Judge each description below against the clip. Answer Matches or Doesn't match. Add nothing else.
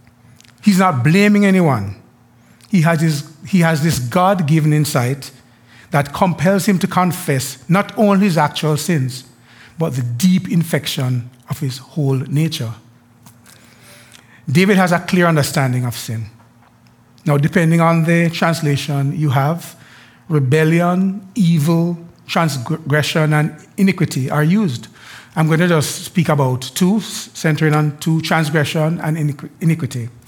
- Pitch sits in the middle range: Matches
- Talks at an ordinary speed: Doesn't match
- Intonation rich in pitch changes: Doesn't match